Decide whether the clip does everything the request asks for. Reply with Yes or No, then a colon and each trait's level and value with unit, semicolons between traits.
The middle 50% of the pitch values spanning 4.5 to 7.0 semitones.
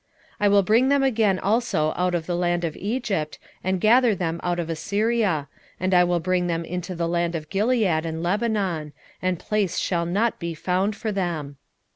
No: average, 3.8 semitones